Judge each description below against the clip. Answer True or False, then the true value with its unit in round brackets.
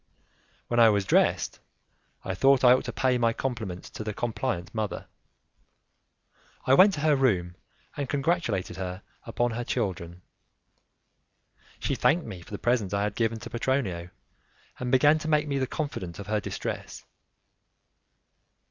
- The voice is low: True (115 Hz)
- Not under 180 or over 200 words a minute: False (155 wpm)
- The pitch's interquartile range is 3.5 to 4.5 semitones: False (5.5 semitones)